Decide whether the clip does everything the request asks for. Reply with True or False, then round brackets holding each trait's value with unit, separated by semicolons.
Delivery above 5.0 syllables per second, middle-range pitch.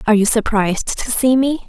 False (6.1 syllables/s; 230 Hz)